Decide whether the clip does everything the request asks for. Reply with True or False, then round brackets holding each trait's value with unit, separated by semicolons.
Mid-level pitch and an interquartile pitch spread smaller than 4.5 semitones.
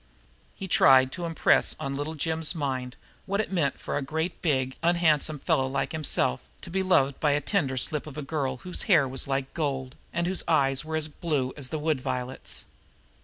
True (145 Hz; 3.4 semitones)